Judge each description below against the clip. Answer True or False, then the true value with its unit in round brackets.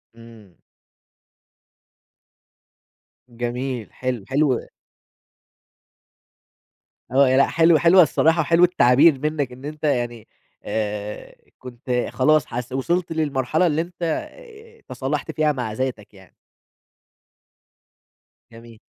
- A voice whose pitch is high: False (135 Hz)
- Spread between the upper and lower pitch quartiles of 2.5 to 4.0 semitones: False (4.7 semitones)